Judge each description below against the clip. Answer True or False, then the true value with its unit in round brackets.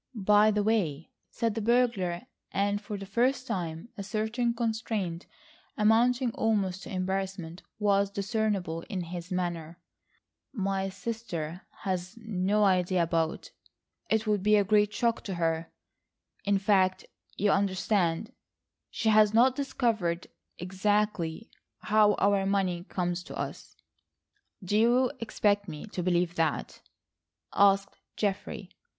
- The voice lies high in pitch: True (200 Hz)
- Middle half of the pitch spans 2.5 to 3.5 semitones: True (3.2 semitones)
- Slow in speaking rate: True (120 wpm)